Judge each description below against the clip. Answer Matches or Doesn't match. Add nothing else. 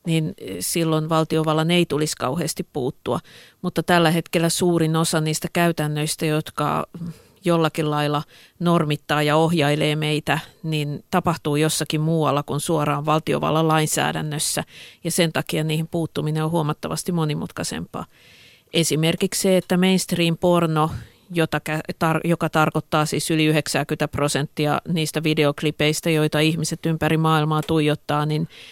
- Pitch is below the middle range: Doesn't match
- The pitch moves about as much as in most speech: Doesn't match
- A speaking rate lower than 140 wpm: Matches